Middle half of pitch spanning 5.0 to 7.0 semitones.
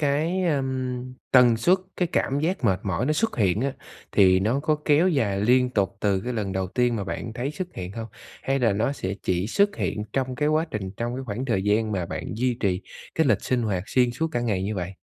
Yes: wide, 5.4 semitones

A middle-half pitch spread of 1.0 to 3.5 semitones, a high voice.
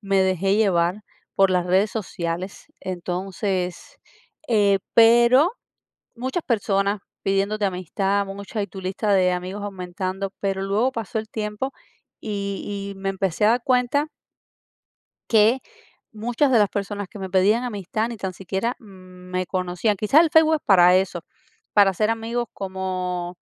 Yes: average, 2.8 semitones; high, 200 Hz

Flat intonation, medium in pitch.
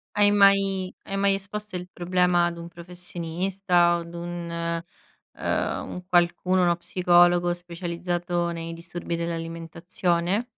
Yes: narrow, 1.3 semitones; medium, 175 Hz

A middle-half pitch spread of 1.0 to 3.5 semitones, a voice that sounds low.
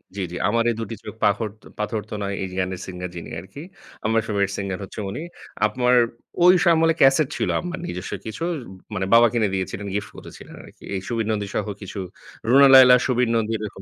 No: average, 4.1 semitones; low, 110 Hz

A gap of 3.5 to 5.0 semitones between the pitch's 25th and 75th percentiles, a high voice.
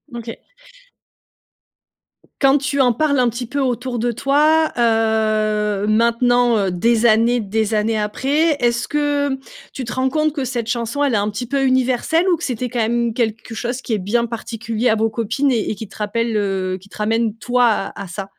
No: average, 3.1 semitones; high, 235 Hz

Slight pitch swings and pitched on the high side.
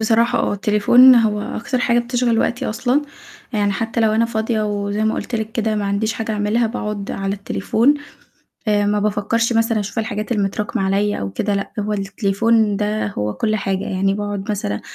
Yes: narrow, 2.1 semitones; high, 215 Hz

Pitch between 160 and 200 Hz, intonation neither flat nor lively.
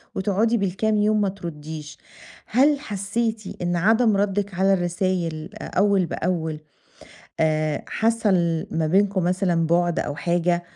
Yes: medium, 185 Hz; average, 3.5 semitones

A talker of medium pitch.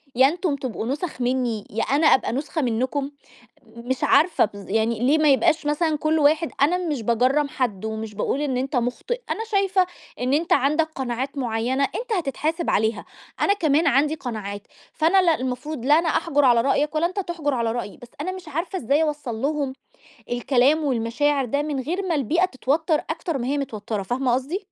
No: very high, 280 Hz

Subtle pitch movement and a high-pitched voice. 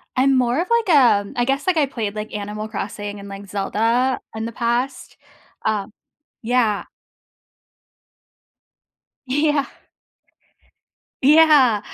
No: average, 4.6 semitones; high, 240 Hz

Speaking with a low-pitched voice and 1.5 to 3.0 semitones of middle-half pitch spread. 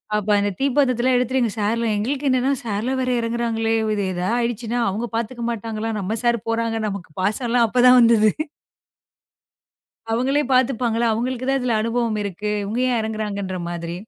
No: high, 230 Hz; narrow, 2.6 semitones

